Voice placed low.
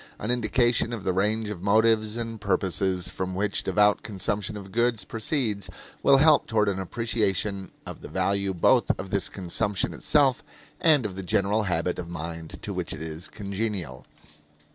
Yes: low, 100 Hz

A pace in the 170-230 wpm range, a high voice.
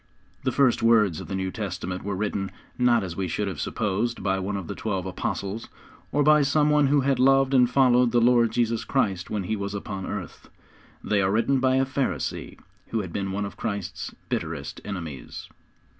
No: average, 200 wpm; low, 105 Hz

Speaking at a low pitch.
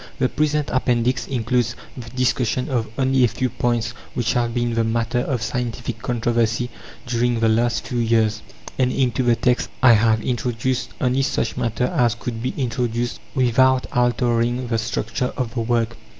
Yes: low, 120 Hz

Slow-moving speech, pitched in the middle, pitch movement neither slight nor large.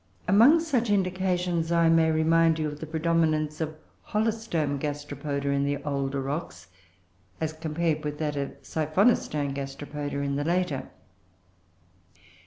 Yes: slow, 130 wpm; medium, 155 Hz; average, 3.0 semitones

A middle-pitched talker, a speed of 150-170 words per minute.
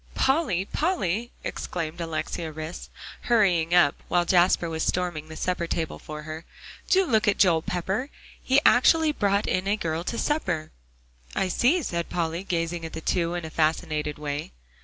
Yes: medium, 175 Hz; average, 165 wpm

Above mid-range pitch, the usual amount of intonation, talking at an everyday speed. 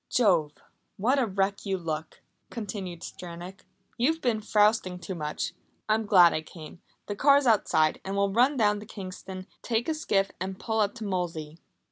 Yes: high, 195 Hz; average, 3.8 semitones; average, 170 wpm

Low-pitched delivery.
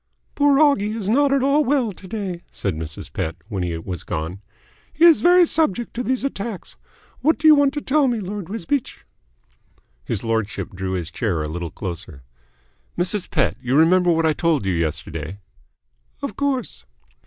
No: medium, 180 Hz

